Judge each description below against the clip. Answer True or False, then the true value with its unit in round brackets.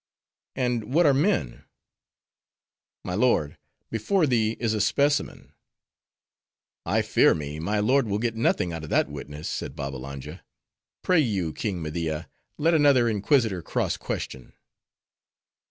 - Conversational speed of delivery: False (130 wpm)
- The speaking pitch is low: True (105 Hz)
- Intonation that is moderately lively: False (8.5 semitones)